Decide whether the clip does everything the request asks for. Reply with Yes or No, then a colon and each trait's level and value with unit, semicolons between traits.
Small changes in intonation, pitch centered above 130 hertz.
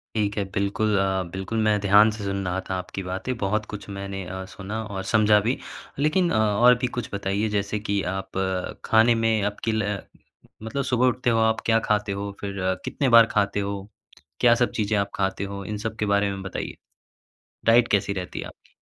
No: narrow, 2.2 semitones; low, 105 Hz